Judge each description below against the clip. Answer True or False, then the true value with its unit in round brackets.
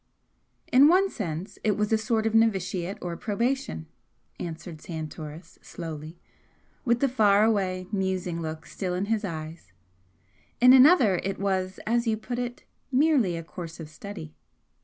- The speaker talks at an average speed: True (150 wpm)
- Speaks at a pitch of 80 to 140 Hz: False (195 Hz)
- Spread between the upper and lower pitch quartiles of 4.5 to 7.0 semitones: True (5.1 semitones)